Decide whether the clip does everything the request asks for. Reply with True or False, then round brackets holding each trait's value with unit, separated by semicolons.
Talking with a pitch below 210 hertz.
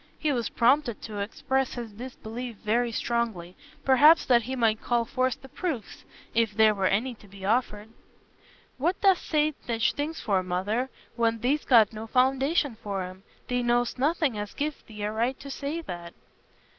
False (235 Hz)